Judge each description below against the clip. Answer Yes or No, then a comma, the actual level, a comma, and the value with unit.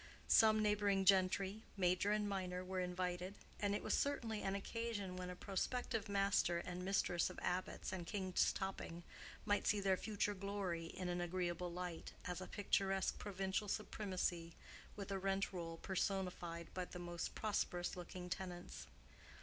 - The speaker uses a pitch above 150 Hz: Yes, high, 190 Hz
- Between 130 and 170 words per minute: Yes, average, 155 wpm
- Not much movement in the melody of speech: Yes, narrow, 2.1 semitones